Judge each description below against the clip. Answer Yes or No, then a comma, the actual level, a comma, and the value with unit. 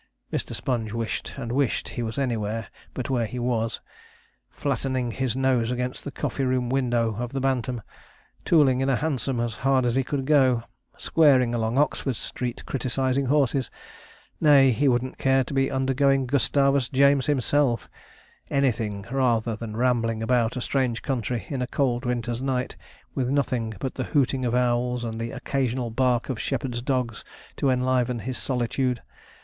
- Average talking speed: Yes, average, 165 wpm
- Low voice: Yes, low, 125 Hz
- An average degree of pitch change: No, narrow, 2.2 semitones